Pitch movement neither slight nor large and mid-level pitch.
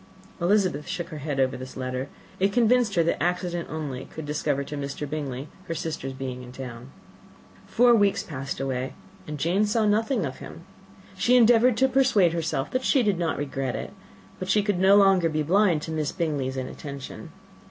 No: wide, 6.7 semitones; medium, 160 Hz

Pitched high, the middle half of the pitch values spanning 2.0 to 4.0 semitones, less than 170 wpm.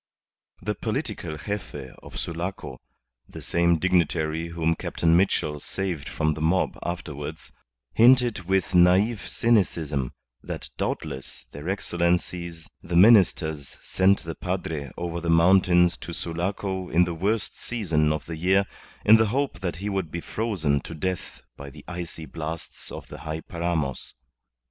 No: very low, 85 Hz; average, 3.2 semitones; average, 145 wpm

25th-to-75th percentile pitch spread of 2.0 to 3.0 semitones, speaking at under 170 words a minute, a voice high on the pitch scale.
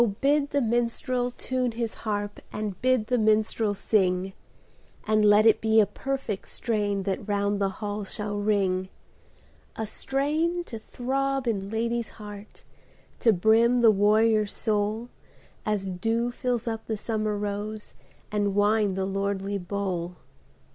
Yes: narrow, 2.5 semitones; average, 140 wpm; high, 215 Hz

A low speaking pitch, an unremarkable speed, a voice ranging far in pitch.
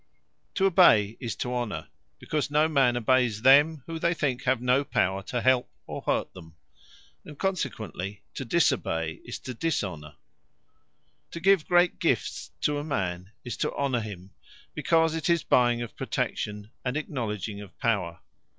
Yes: low, 125 Hz; average, 155 wpm; wide, 6.4 semitones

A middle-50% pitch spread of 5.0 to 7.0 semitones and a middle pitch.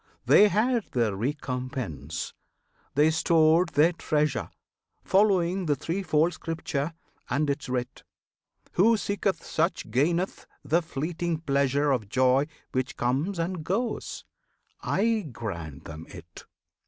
Yes: wide, 5.4 semitones; medium, 155 Hz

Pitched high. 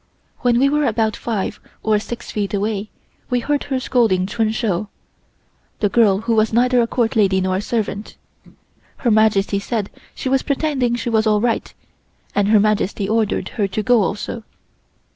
Yes: high, 220 Hz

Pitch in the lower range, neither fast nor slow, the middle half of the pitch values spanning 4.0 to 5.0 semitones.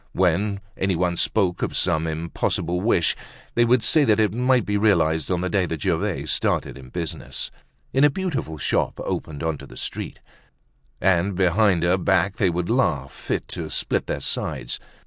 Yes: very low, 90 Hz; average, 175 wpm; average, 4.3 semitones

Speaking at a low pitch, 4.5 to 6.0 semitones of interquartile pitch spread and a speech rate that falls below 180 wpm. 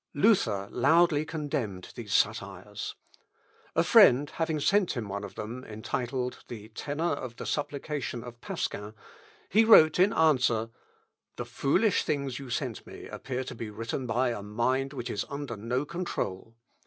Yes: low, 125 Hz; average, 4.8 semitones; average, 155 wpm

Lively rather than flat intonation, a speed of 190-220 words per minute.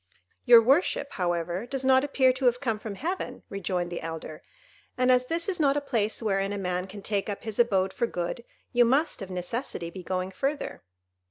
Yes: wide, 5.8 semitones; average, 200 wpm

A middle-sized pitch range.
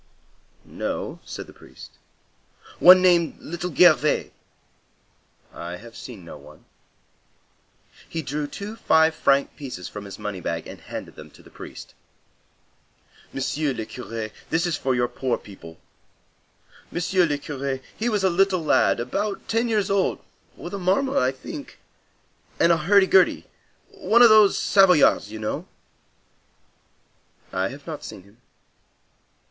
No: wide, 8.2 semitones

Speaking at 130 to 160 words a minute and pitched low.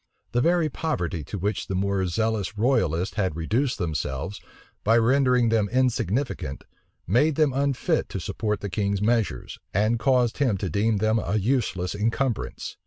Yes: average, 155 wpm; low, 110 Hz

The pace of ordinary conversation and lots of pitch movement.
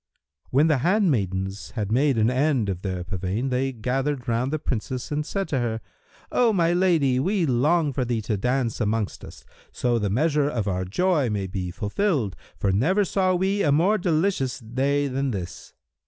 Yes: average, 185 wpm; wide, 6.4 semitones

